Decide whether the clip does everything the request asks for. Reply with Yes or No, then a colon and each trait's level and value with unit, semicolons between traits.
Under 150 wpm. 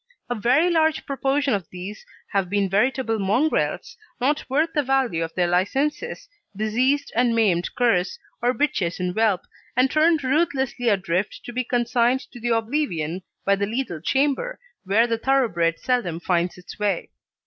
No: average, 155 wpm